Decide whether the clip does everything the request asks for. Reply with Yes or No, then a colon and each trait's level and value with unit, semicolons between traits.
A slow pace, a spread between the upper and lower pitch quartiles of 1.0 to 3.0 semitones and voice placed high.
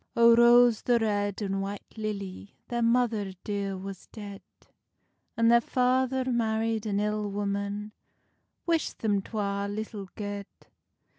Yes: slow, 130 wpm; narrow, 2.6 semitones; high, 210 Hz